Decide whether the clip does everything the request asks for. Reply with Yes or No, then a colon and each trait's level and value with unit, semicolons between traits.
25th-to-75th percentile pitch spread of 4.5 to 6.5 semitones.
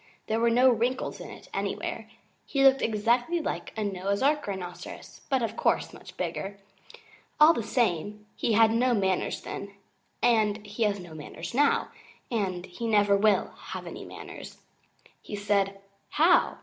No: average, 3.4 semitones